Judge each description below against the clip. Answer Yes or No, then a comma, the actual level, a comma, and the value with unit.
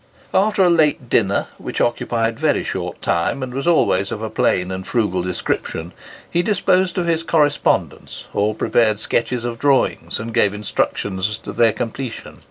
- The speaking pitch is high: No, low, 115 Hz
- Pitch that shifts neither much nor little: No, wide, 6.2 semitones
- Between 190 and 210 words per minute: No, average, 170 wpm